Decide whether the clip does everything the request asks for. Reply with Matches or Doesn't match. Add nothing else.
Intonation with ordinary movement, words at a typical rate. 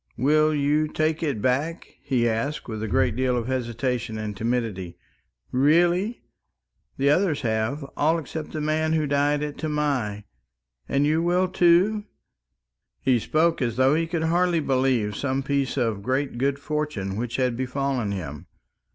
Matches